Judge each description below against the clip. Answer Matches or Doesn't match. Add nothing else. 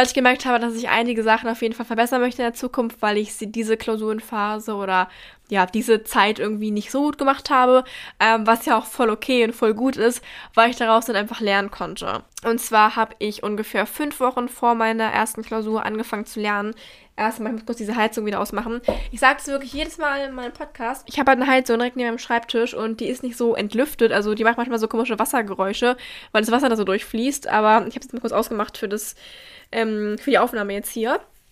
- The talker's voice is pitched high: Matches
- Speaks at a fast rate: Matches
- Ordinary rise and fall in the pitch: Doesn't match